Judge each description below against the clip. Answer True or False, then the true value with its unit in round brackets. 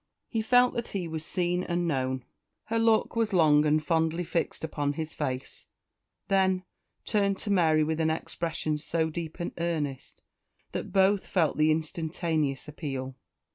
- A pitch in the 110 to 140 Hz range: False (160 Hz)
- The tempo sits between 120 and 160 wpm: True (155 wpm)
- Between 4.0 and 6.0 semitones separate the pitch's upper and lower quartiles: False (3.4 semitones)